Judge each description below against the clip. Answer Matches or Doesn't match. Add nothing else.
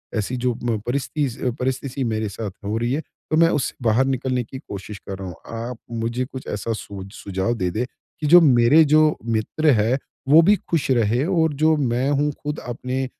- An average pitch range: Matches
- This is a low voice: Matches